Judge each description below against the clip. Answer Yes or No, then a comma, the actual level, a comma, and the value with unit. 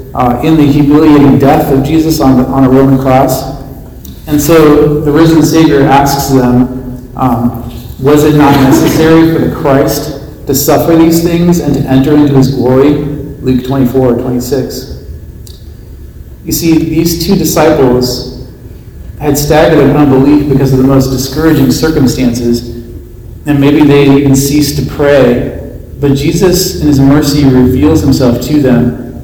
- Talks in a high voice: No, medium, 140 Hz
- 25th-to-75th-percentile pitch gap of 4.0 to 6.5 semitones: No, average, 2.7 semitones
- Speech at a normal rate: Yes, average, 150 wpm